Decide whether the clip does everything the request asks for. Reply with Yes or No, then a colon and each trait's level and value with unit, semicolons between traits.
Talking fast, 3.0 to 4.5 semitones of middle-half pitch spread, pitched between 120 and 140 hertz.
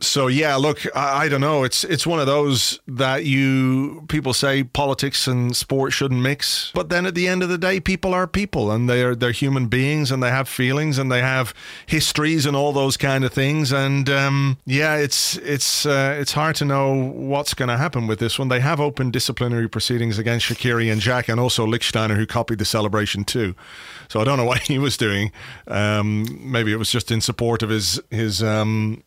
Yes: fast, 215 wpm; average, 3.3 semitones; low, 130 Hz